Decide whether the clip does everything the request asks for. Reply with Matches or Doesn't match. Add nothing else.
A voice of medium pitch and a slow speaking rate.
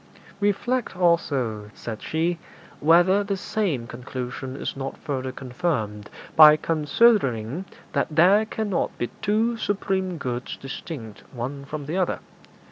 Matches